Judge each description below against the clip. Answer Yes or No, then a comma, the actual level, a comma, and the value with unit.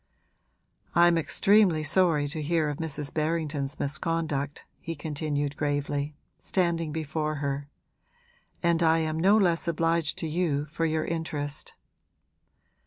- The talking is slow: Yes, slow, 120 wpm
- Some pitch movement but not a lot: No, narrow, 2.3 semitones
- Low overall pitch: No, medium, 155 Hz